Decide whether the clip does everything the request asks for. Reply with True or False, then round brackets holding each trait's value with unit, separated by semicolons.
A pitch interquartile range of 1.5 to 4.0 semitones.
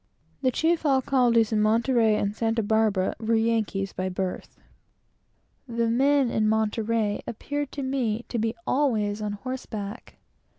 True (3.2 semitones)